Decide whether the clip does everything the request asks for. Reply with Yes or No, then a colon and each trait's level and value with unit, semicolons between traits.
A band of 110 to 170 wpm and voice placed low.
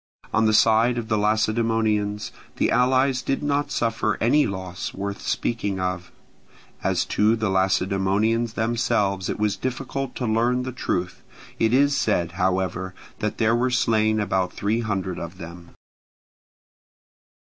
Yes: average, 140 wpm; low, 110 Hz